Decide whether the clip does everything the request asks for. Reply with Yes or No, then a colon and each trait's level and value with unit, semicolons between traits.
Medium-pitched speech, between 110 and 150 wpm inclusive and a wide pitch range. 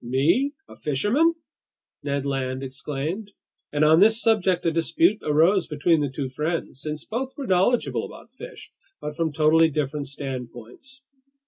Yes: medium, 155 Hz; average, 145 wpm; wide, 5.7 semitones